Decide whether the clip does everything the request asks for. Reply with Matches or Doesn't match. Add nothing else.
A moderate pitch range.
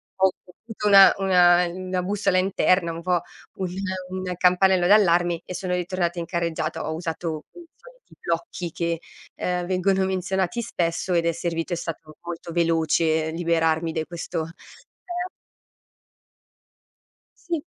Doesn't match